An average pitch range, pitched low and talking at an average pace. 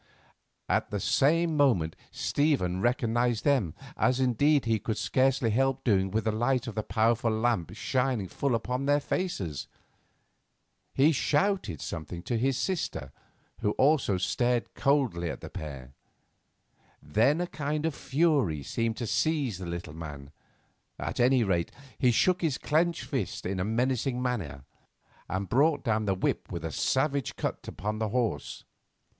No: wide, 6.5 semitones; low, 120 Hz; average, 150 wpm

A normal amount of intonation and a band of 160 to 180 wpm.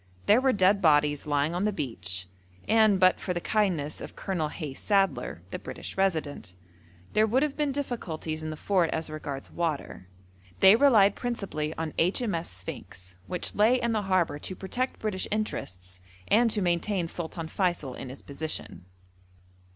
No: wide, 5.8 semitones; average, 165 wpm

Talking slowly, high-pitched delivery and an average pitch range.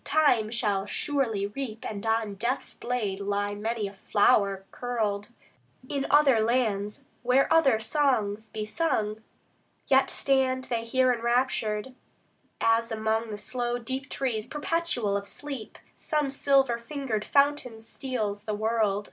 Yes: slow, 130 wpm; high, 230 Hz; average, 3.8 semitones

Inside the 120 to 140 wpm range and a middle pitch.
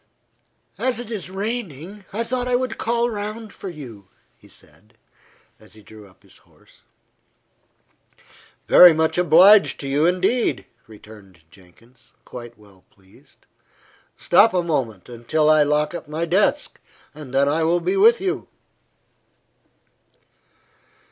Yes: slow, 135 wpm; medium, 160 Hz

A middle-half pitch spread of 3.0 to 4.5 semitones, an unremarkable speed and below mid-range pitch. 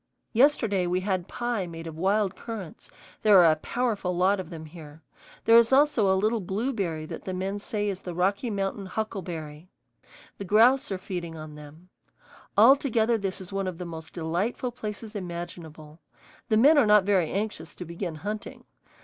No: average, 4.2 semitones; average, 175 wpm; high, 190 Hz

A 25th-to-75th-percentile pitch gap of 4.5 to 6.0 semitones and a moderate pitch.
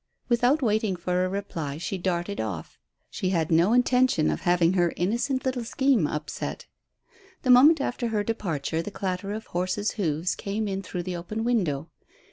No: average, 5.0 semitones; high, 195 Hz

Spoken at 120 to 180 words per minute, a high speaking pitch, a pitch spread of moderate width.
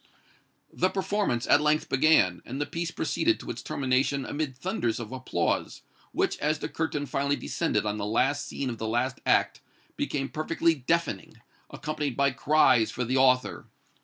No: average, 165 wpm; medium, 140 Hz; average, 3.7 semitones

